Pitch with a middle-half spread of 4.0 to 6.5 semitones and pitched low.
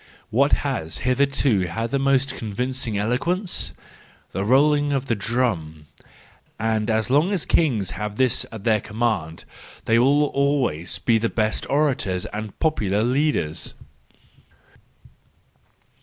Yes: average, 4.7 semitones; low, 120 Hz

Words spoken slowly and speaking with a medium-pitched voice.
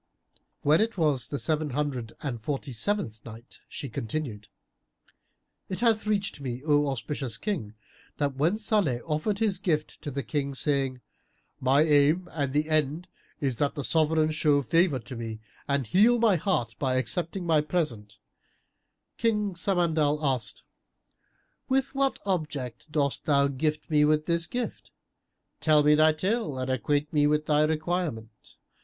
No: average, 150 wpm; medium, 150 Hz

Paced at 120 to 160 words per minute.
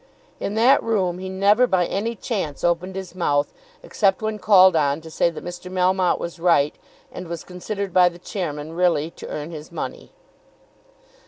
No: average, 175 wpm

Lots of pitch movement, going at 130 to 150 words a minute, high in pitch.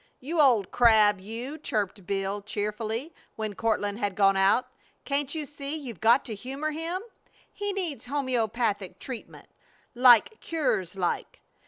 Yes: wide, 5.7 semitones; average, 140 wpm; high, 235 Hz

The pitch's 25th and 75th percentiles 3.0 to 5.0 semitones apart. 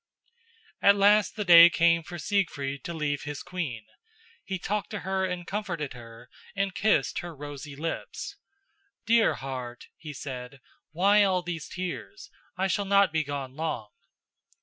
No: wide, 5.4 semitones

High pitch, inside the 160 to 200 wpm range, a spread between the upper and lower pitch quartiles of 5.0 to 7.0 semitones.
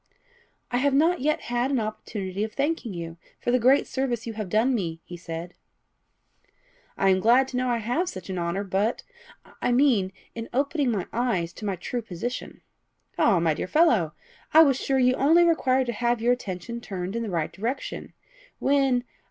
Yes: high, 235 Hz; average, 195 wpm; wide, 5.6 semitones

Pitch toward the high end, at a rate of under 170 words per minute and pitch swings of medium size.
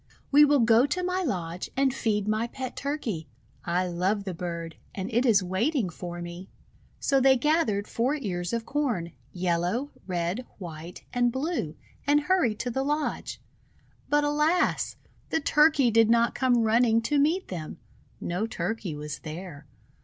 No: high, 225 Hz; average, 160 wpm; wide, 7.8 semitones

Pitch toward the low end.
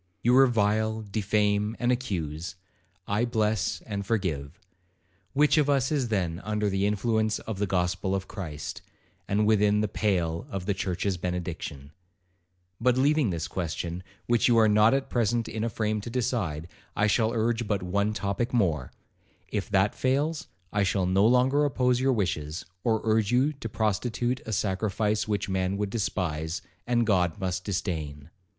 Yes: low, 105 Hz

